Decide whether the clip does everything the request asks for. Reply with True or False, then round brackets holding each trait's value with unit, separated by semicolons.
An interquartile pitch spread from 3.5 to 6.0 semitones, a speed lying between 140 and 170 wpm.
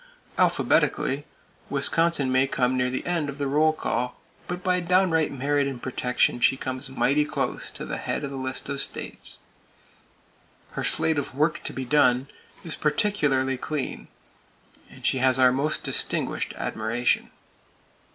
False (3.0 semitones; 150 wpm)